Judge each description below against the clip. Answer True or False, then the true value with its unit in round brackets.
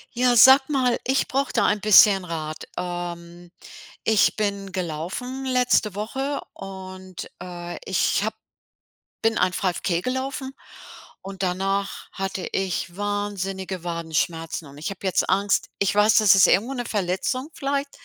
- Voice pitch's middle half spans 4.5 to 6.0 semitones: True (5.0 semitones)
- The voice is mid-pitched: False (195 Hz)